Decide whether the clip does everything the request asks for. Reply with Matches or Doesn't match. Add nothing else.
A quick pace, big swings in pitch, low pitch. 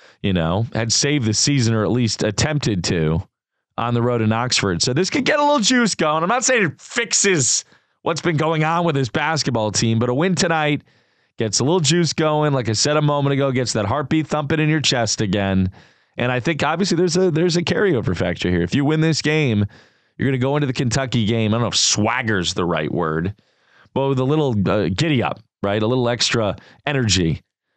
Matches